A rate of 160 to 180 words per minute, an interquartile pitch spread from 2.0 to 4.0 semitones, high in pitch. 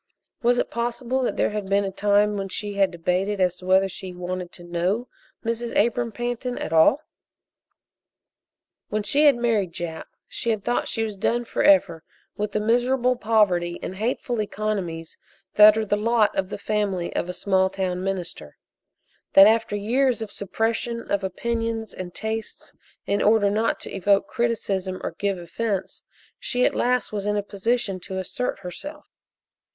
Yes: average, 170 wpm; average, 3.6 semitones; high, 205 Hz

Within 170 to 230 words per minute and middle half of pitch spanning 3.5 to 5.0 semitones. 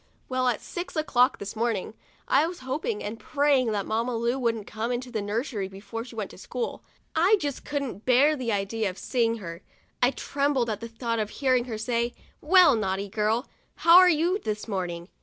Yes: average, 200 wpm; average, 4.3 semitones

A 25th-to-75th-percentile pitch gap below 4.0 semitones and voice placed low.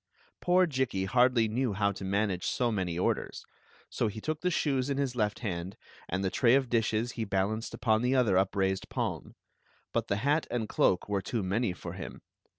No: average, 4.6 semitones; low, 110 Hz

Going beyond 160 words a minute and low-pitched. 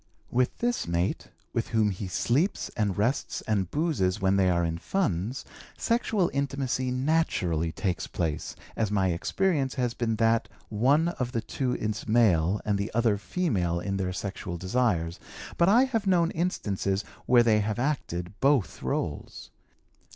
No: average, 155 wpm; low, 110 Hz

